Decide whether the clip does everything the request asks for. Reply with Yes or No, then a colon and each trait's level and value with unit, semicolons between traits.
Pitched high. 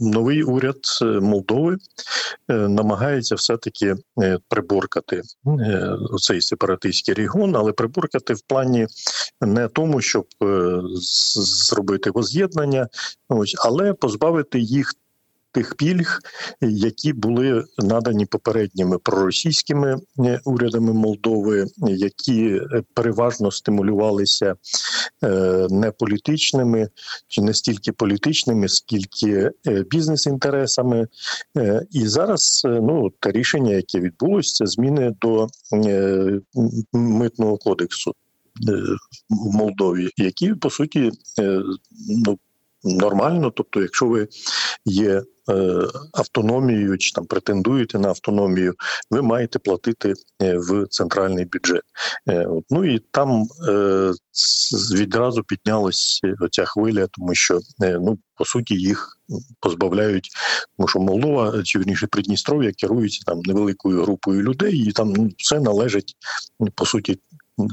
No: low, 110 Hz